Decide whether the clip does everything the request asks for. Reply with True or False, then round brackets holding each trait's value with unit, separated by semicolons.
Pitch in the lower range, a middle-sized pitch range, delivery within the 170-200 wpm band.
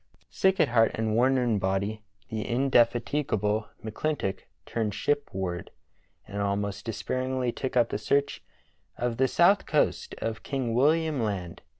False (115 Hz; 4.2 semitones; 135 wpm)